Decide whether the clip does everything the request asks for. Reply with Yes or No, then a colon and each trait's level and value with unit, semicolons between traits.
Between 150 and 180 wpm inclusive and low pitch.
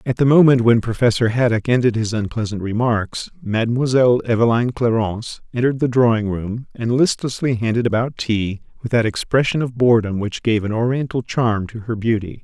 Yes: average, 170 wpm; low, 115 Hz